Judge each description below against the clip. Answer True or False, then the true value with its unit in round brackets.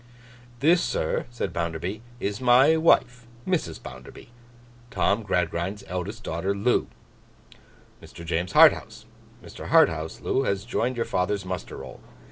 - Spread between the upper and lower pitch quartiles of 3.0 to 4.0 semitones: False (5.6 semitones)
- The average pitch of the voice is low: True (100 Hz)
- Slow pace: True (120 wpm)